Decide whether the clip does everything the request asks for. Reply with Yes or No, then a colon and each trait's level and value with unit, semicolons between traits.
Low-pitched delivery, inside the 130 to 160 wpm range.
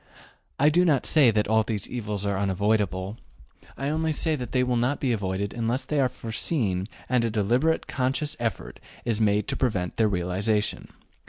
No: low, 115 Hz; average, 180 wpm